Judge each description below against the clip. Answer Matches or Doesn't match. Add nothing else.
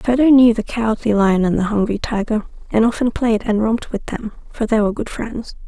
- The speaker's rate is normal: Doesn't match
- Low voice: Doesn't match